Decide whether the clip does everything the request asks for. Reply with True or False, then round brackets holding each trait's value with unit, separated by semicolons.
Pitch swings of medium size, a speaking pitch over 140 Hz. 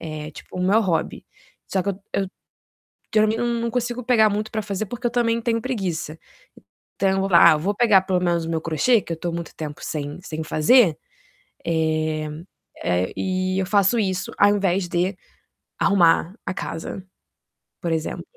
True (4.7 semitones; 185 Hz)